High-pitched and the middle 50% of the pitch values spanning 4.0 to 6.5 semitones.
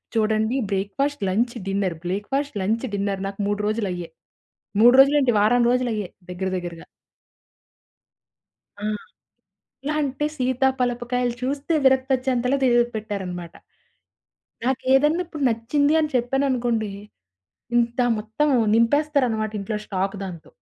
Yes: high, 235 Hz; average, 4.6 semitones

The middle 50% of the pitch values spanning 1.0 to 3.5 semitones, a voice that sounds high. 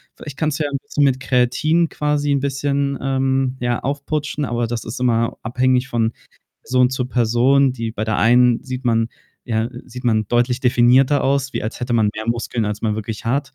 No: average, 2.8 semitones; low, 125 Hz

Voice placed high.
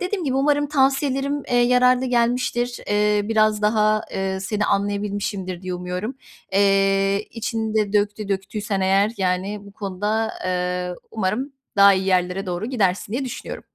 Yes: high, 210 Hz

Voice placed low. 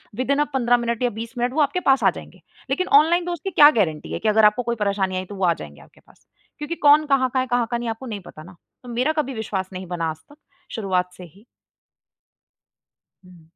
No: high, 235 Hz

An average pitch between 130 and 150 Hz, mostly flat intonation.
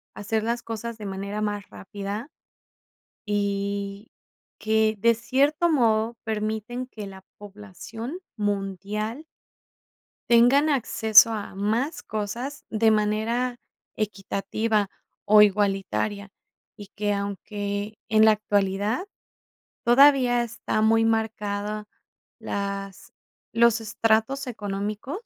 No: high, 215 Hz; narrow, 2.3 semitones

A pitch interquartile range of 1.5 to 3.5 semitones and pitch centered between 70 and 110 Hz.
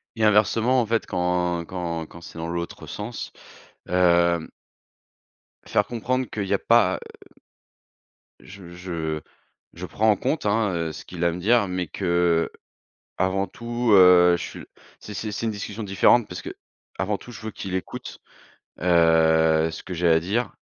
No: average, 3.9 semitones; very low, 90 Hz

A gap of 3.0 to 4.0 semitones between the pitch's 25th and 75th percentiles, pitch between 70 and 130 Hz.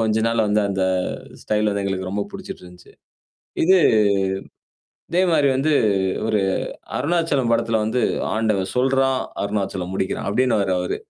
No: average, 4.9 semitones; low, 110 Hz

